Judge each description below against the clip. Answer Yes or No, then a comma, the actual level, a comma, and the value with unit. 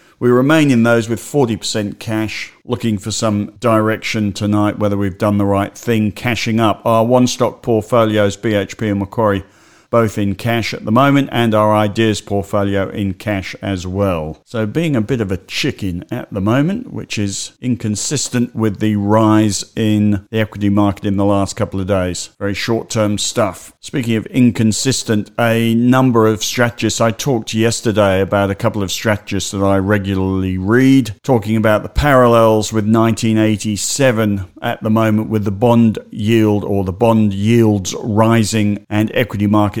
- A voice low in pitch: Yes, low, 110 Hz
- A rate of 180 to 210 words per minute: No, average, 165 wpm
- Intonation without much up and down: Yes, narrow, 2.2 semitones